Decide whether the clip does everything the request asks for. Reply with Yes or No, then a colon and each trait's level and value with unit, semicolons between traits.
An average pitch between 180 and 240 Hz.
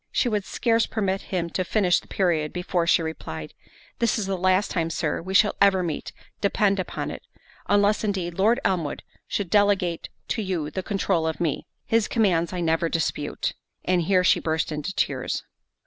Yes: medium, 185 Hz